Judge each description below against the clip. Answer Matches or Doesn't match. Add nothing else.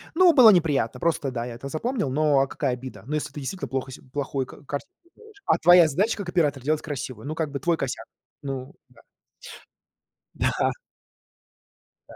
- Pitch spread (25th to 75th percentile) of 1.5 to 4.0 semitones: Doesn't match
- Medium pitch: Matches